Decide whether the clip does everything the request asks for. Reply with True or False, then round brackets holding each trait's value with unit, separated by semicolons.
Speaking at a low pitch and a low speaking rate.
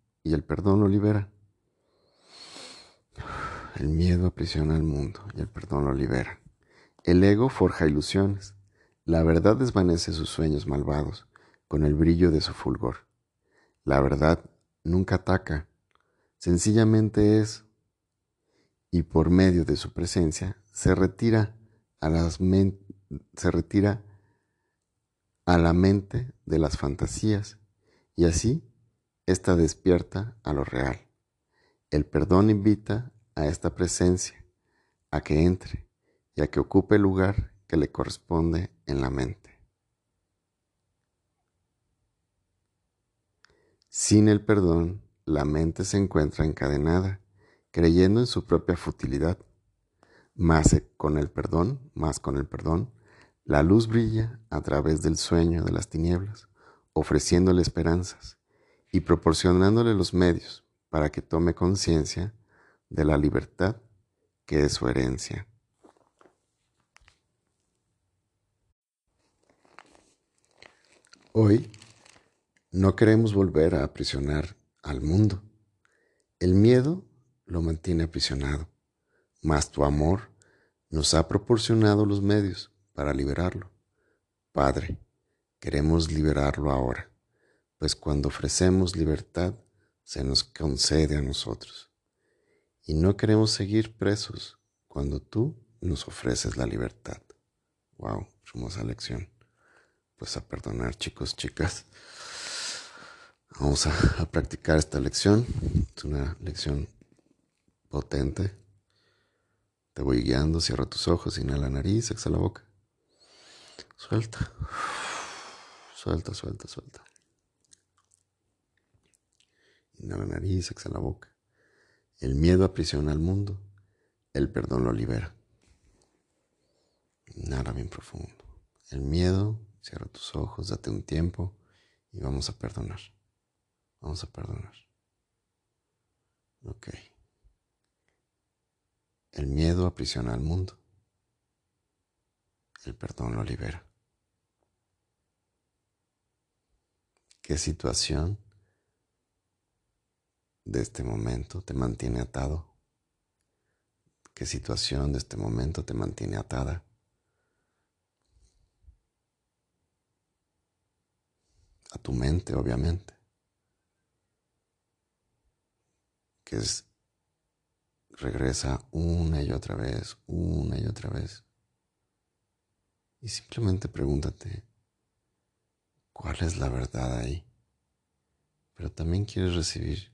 True (90 Hz; 100 wpm)